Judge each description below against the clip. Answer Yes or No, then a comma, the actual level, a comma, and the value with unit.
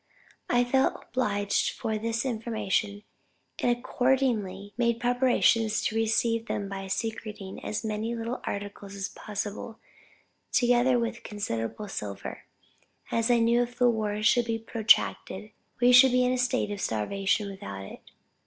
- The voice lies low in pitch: No, high, 225 Hz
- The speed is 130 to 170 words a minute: Yes, average, 145 wpm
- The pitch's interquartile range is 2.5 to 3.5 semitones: Yes, average, 3.0 semitones